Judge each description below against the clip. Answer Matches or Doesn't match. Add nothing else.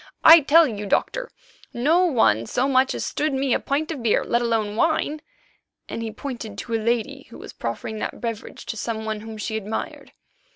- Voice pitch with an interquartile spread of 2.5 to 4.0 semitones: Doesn't match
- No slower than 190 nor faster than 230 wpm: Matches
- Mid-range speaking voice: Doesn't match